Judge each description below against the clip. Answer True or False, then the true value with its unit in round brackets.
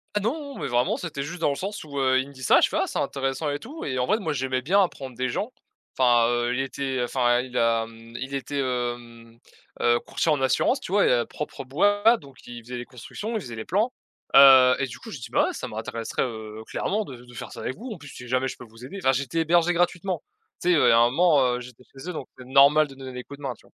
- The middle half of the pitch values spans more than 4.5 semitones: True (5.0 semitones)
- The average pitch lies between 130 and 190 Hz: True (135 Hz)